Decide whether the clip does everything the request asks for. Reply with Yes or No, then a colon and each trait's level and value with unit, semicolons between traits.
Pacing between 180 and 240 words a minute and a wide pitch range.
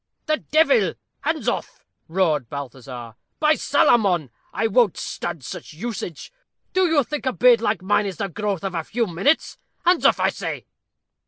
No: average, 165 wpm; wide, 7.9 semitones